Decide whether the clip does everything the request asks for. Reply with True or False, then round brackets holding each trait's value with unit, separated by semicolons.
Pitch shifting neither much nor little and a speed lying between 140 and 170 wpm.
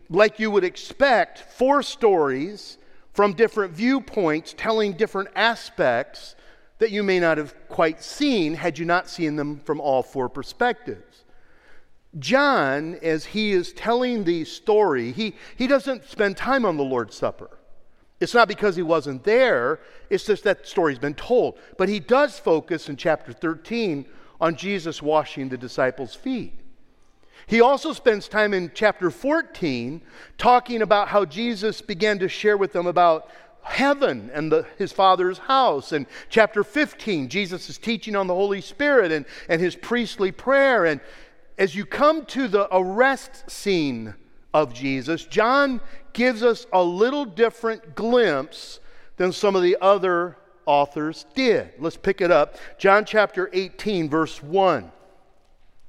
False (6.6 semitones; 150 wpm)